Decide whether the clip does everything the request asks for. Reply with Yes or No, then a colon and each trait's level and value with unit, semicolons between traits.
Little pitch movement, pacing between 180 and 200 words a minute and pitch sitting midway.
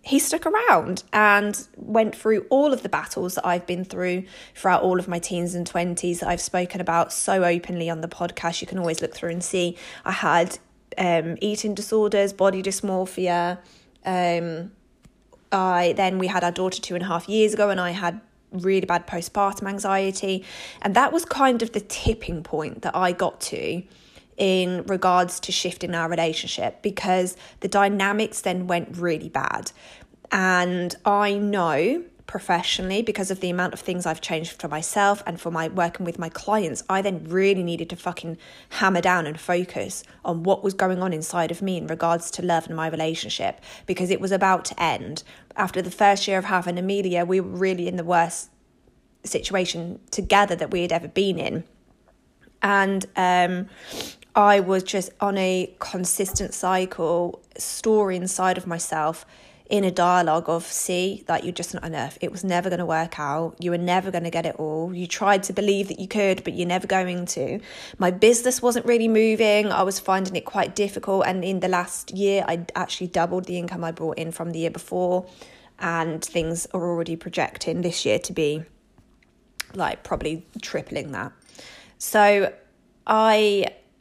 Yes: narrow, 2.3 semitones; average, 185 wpm; medium, 180 Hz